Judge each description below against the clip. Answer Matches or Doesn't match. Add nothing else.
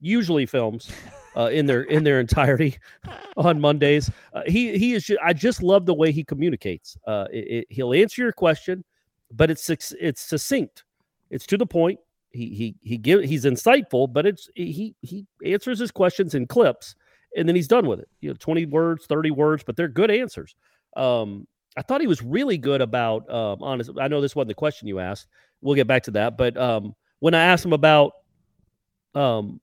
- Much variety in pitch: Matches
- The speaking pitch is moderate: Matches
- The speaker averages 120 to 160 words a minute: Doesn't match